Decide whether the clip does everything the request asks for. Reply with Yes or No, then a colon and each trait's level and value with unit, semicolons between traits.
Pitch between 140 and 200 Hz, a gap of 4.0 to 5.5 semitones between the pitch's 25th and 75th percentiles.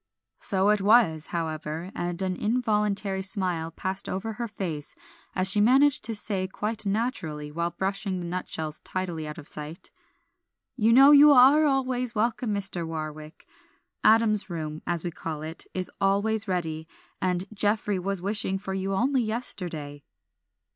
Yes: high, 190 Hz; average, 4.6 semitones